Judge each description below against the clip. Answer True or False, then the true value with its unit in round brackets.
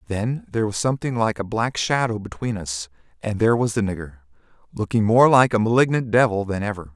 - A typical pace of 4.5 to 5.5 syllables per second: False (6.1 syllables/s)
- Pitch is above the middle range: False (110 Hz)